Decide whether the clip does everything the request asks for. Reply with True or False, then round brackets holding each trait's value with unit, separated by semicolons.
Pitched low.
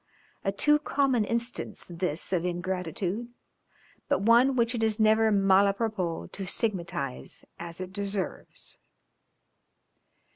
False (200 Hz)